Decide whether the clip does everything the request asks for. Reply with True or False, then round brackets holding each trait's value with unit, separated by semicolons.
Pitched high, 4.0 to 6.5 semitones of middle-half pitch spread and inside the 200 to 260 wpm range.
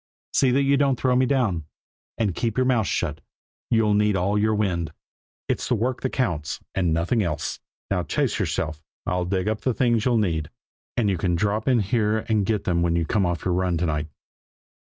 False (105 Hz; 5.2 semitones; 205 wpm)